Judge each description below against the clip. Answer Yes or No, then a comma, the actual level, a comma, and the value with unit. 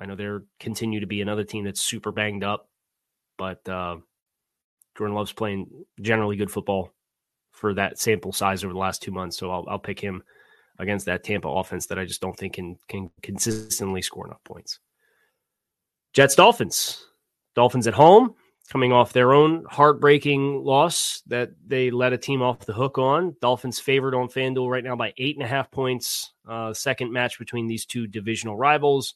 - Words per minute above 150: Yes, average, 185 wpm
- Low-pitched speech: Yes, low, 115 Hz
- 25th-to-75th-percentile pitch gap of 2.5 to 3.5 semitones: No, average, 4.3 semitones